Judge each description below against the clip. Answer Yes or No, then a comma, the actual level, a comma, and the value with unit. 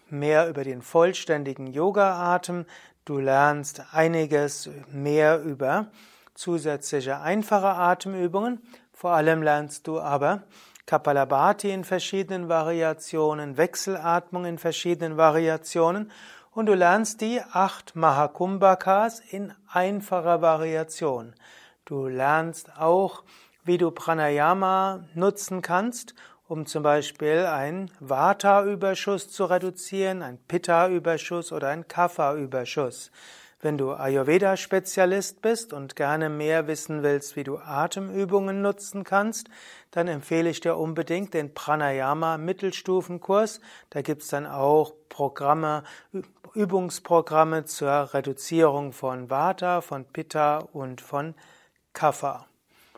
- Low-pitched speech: No, medium, 165 Hz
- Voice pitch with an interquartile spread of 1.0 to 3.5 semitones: No, average, 4.2 semitones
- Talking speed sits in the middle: No, slow, 105 wpm